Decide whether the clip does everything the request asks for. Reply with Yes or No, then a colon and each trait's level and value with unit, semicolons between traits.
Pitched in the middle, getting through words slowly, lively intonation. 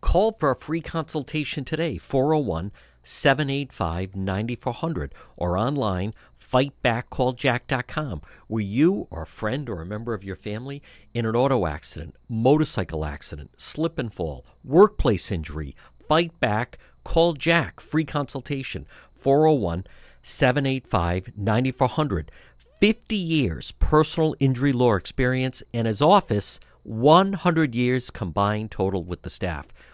No: low, 125 Hz; slow, 120 wpm; wide, 7.3 semitones